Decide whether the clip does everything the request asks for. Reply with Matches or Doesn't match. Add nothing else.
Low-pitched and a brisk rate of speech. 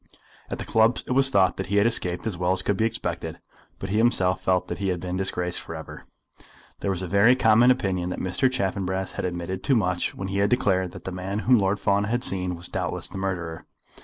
Matches